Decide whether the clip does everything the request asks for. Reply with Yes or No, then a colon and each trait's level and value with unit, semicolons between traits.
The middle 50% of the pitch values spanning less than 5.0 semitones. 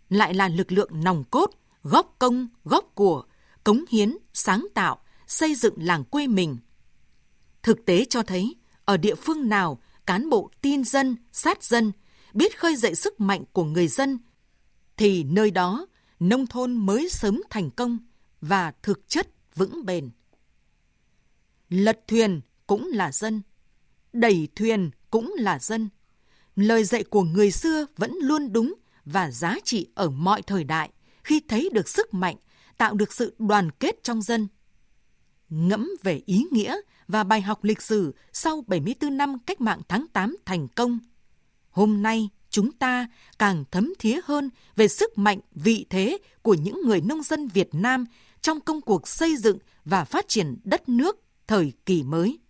Yes: average, 4.6 semitones